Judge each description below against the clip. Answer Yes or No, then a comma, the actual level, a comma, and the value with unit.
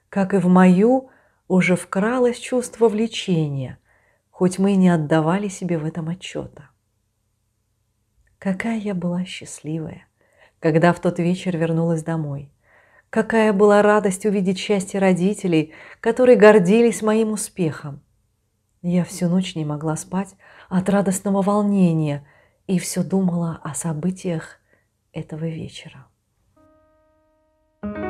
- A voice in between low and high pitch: Yes, medium, 180 Hz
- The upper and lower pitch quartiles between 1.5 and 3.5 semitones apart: No, average, 4.7 semitones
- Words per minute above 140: No, average, 115 wpm